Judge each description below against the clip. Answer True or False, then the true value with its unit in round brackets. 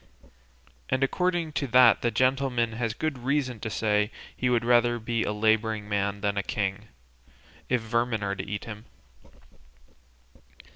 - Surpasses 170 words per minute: False (150 wpm)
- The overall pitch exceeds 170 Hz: False (115 Hz)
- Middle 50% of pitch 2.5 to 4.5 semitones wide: True (3.3 semitones)